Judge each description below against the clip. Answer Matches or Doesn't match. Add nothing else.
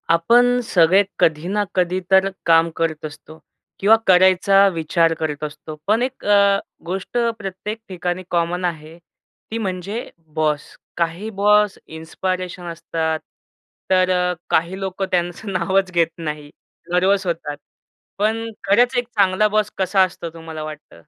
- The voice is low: Doesn't match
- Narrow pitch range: Doesn't match